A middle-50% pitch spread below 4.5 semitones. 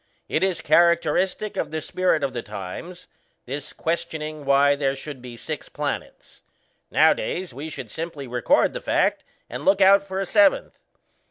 No: average, 4.8 semitones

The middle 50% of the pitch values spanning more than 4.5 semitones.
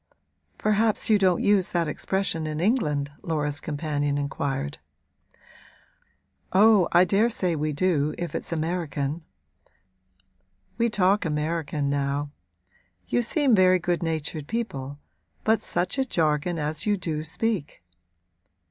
Yes: average, 4.9 semitones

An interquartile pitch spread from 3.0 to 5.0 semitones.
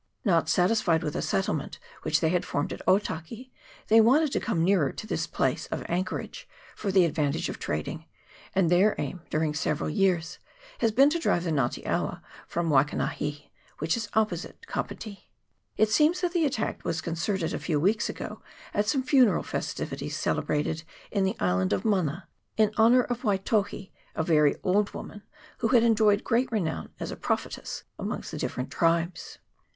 No: wide, 5.4 semitones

